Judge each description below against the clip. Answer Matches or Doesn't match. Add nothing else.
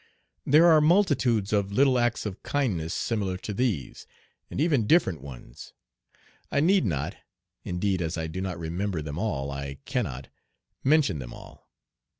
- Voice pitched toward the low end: Matches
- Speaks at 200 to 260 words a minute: Doesn't match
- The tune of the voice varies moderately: Doesn't match